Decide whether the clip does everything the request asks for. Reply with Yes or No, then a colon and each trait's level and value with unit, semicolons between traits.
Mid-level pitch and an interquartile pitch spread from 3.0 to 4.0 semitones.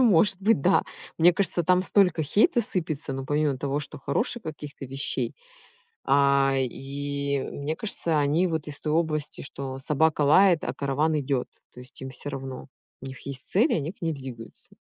Yes: medium, 145 Hz; average, 3.5 semitones